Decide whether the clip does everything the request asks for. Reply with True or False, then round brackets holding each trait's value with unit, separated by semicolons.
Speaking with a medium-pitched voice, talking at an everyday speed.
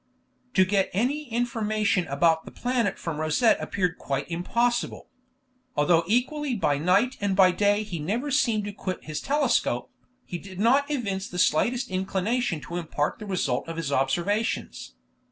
False (195 Hz; 155 wpm)